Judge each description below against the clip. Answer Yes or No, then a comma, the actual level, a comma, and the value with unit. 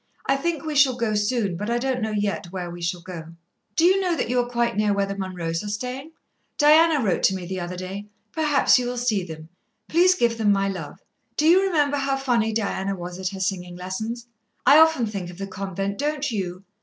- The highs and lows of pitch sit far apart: Yes, wide, 6.4 semitones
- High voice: Yes, high, 210 Hz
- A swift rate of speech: Yes, fast, 230 wpm